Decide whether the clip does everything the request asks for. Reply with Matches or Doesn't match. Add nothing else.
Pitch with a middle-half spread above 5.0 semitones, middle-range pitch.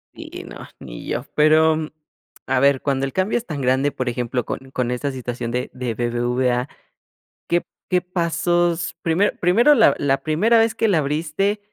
Matches